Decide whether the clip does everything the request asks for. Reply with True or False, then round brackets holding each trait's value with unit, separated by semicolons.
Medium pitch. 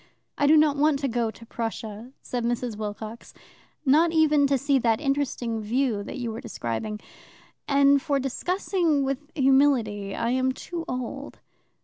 False (260 Hz)